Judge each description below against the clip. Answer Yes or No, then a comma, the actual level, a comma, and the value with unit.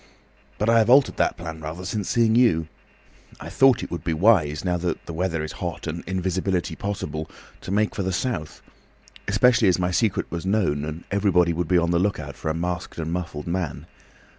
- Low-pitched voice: Yes, very low, 90 Hz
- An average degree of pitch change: Yes, average, 3.7 semitones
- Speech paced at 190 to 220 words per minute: Yes, average, 200 wpm